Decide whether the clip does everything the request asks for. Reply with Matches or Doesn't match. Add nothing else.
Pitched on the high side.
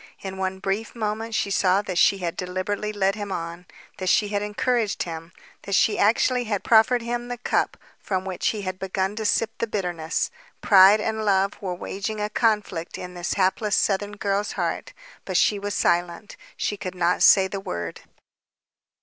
Matches